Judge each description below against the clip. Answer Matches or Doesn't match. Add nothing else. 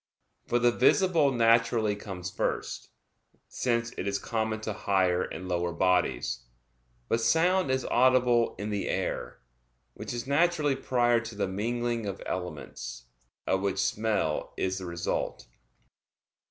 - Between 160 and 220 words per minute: Doesn't match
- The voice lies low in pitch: Matches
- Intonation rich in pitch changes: Doesn't match